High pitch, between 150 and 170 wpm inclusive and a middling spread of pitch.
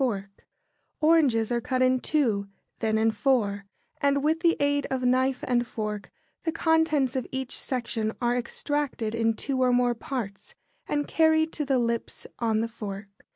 Yes: very high, 250 Hz; average, 165 wpm; average, 4.1 semitones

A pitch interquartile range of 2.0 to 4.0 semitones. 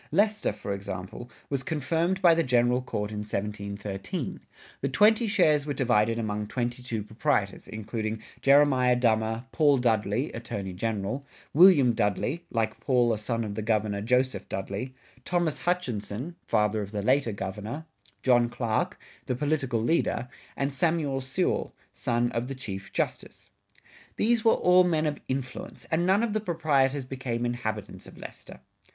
No: average, 5.3 semitones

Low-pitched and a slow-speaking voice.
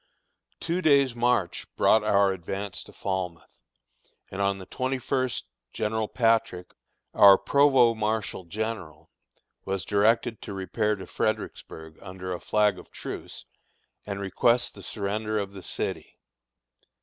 Yes: low, 105 Hz; slow, 130 wpm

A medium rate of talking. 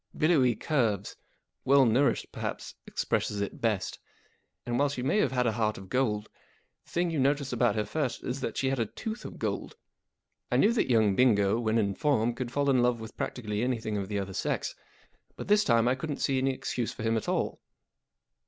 No: fast, 210 wpm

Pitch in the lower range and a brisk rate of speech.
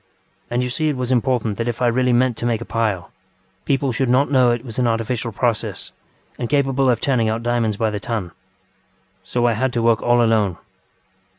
Yes: low, 120 Hz; fast, 210 wpm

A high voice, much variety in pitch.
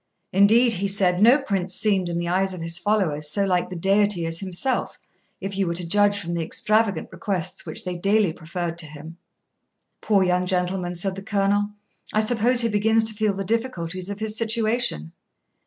No: high, 195 Hz; average, 3.3 semitones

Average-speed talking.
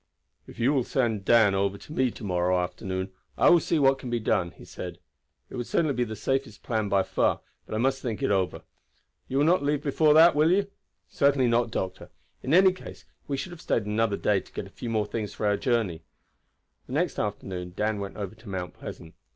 No: fast, 225 wpm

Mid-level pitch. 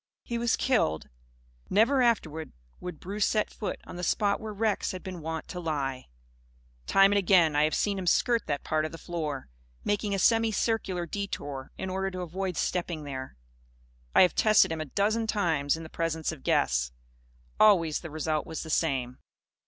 Yes: medium, 175 Hz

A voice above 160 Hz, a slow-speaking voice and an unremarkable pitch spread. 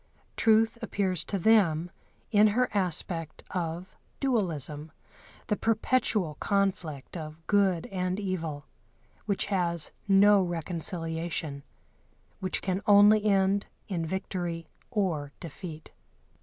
Yes: medium, 185 Hz; slow, 100 wpm; average, 3.7 semitones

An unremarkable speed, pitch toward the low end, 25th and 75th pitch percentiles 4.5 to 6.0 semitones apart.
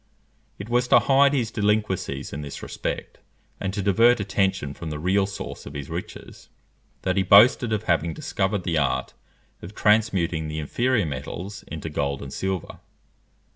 Yes: average, 165 wpm; very low, 95 Hz; average, 5.3 semitones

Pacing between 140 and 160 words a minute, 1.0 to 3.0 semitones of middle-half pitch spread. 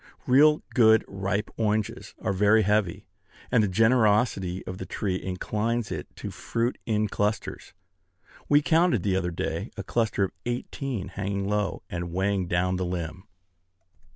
No: average, 150 wpm; average, 3.4 semitones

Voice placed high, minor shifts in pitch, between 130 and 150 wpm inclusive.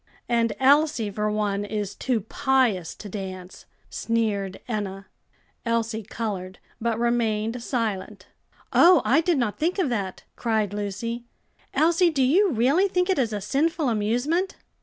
No: high, 230 Hz; average, 4.8 semitones; average, 140 wpm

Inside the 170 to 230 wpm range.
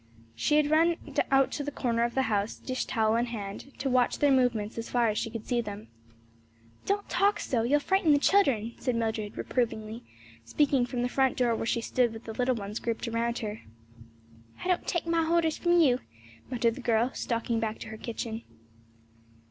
Yes: average, 195 wpm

